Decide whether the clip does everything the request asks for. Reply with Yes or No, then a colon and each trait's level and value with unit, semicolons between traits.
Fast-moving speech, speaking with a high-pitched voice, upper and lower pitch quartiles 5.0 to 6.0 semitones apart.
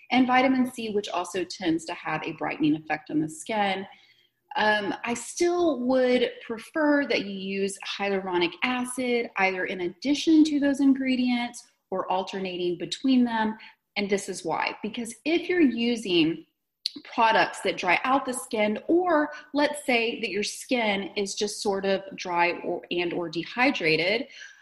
No: average, 150 wpm; high, 225 Hz; wide, 5.5 semitones